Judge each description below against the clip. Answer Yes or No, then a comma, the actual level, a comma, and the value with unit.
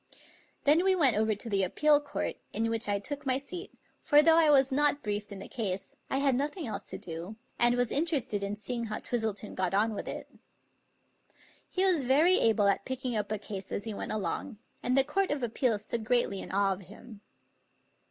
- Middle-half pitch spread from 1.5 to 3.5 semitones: No, wide, 5.6 semitones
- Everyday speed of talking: No, fast, 215 wpm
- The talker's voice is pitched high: Yes, high, 235 Hz